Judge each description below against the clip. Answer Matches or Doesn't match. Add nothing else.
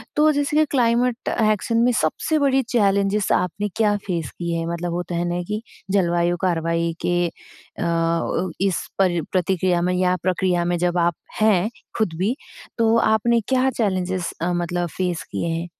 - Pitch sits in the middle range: Matches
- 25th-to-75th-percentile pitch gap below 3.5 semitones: Doesn't match